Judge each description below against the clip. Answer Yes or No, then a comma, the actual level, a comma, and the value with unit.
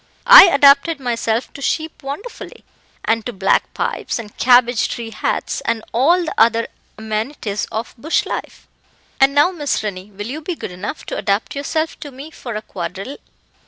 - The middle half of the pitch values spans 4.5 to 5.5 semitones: Yes, average, 5.2 semitones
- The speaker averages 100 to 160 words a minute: No, average, 170 wpm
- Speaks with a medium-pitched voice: No, high, 245 Hz